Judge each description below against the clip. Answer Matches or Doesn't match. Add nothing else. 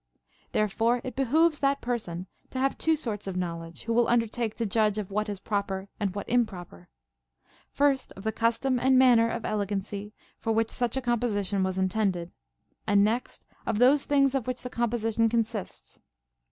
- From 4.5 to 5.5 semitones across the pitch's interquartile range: Doesn't match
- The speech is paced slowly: Doesn't match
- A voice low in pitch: Doesn't match